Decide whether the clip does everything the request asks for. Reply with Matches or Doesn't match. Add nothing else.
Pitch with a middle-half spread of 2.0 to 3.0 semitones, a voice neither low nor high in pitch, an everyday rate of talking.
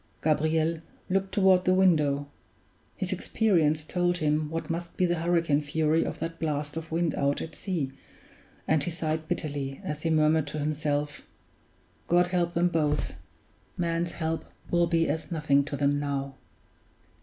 Matches